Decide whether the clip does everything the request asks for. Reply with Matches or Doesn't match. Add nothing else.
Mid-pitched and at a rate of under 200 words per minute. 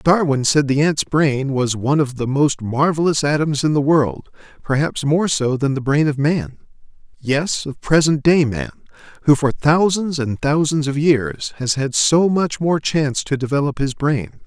Matches